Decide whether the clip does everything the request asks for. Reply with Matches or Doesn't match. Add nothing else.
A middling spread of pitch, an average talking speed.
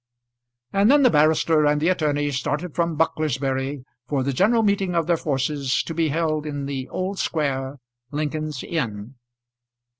Matches